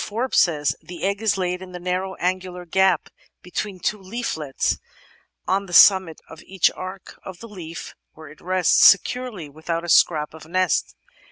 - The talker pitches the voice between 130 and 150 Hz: No, medium, 185 Hz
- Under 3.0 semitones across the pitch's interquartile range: Yes, narrow, 2.4 semitones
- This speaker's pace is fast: No, average, 170 wpm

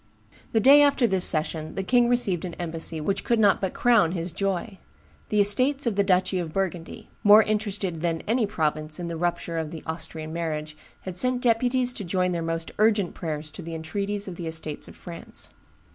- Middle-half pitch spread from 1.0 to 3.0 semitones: No, average, 4.5 semitones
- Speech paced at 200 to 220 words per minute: Yes, fast, 205 wpm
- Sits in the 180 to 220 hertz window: Yes, medium, 185 Hz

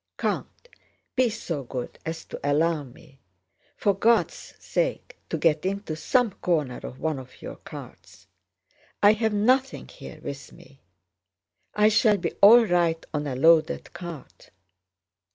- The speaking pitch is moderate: Yes, medium, 170 Hz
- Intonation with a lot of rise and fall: Yes, wide, 6.7 semitones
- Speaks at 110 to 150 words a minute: Yes, average, 140 wpm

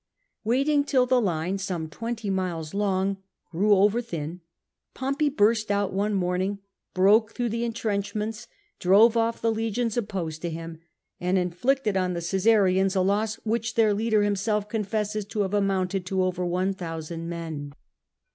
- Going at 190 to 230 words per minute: No, average, 155 wpm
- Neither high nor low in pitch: No, high, 200 Hz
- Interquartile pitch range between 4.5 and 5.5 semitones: No, average, 3.5 semitones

